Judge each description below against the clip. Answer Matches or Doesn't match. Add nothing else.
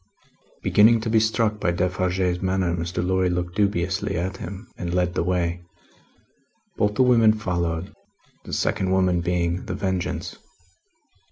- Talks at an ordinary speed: Matches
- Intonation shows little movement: Matches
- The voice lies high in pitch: Doesn't match